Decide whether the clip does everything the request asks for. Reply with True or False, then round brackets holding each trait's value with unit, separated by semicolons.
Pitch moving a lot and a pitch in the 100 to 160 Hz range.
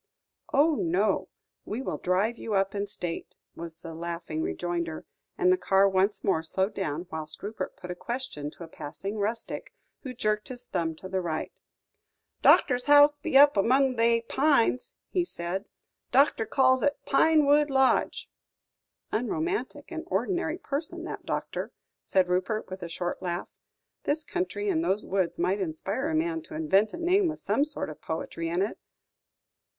False (8.3 semitones; 215 Hz)